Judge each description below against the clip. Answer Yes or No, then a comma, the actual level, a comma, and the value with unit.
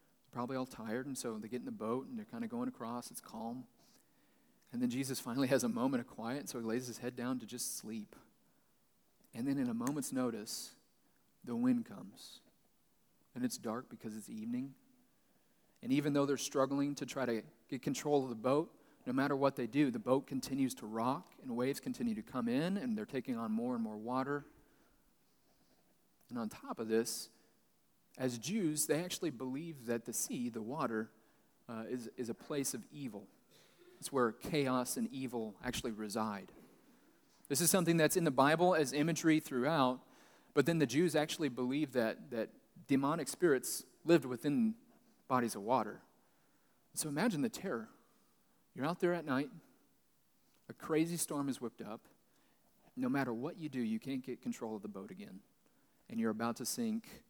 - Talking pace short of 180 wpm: No, average, 185 wpm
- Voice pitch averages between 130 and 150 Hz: Yes, medium, 140 Hz